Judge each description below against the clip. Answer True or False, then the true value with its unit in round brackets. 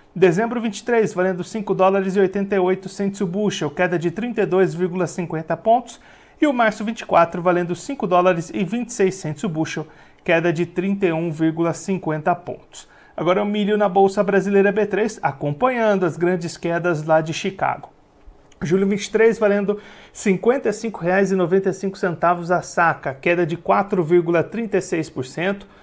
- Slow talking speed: True (110 wpm)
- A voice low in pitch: False (190 Hz)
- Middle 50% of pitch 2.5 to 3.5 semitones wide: True (3.1 semitones)